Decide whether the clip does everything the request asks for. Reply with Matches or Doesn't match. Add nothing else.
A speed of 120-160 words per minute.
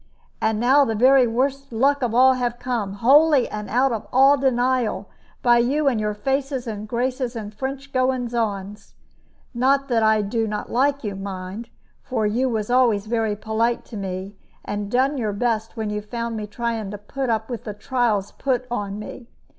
Doesn't match